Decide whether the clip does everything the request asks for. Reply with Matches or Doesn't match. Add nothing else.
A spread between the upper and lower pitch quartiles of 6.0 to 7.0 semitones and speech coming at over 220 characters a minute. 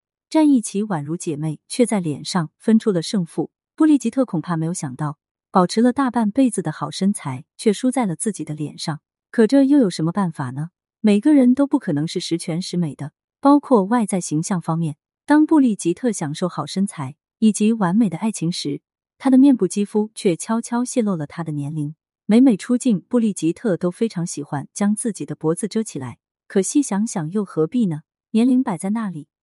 Matches